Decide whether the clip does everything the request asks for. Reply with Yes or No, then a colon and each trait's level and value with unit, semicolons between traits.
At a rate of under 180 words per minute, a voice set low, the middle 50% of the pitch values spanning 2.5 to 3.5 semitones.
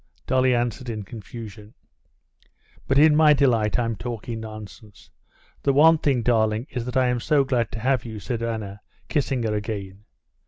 Yes: average, 165 wpm; low, 115 Hz; average, 3.2 semitones